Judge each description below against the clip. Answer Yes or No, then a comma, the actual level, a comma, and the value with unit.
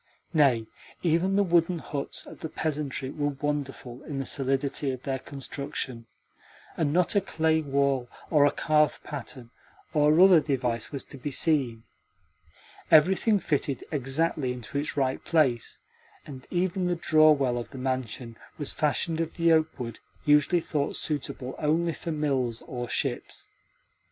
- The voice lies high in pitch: No, medium, 145 Hz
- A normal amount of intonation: Yes, average, 3.4 semitones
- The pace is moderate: Yes, average, 150 wpm